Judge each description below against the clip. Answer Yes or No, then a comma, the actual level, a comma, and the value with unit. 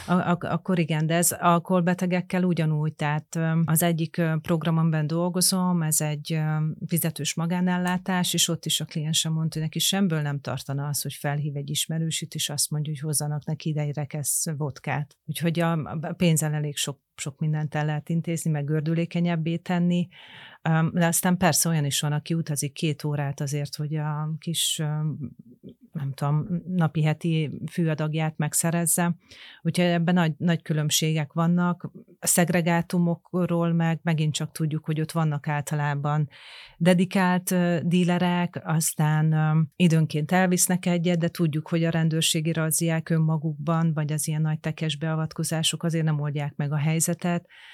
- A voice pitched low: No, medium, 160 Hz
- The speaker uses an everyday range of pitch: No, narrow, 2.0 semitones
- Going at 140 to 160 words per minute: Yes, average, 145 wpm